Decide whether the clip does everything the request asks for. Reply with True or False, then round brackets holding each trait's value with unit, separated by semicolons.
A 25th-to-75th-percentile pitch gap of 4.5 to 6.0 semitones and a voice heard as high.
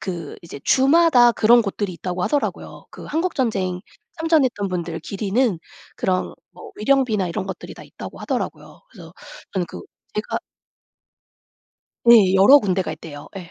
True (5.6 semitones; 200 Hz)